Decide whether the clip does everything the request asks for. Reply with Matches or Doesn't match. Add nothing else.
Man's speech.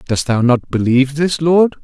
Matches